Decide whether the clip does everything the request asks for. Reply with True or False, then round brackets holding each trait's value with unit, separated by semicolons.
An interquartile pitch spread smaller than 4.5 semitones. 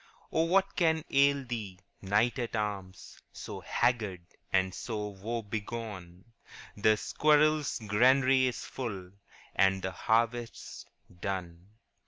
False (5.0 semitones)